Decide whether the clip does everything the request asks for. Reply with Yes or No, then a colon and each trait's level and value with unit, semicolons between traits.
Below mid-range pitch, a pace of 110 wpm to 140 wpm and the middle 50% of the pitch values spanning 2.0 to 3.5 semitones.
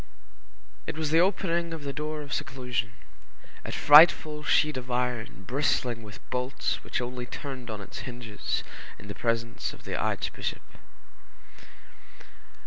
No: low, 125 Hz; slow, 135 wpm; average, 4.1 semitones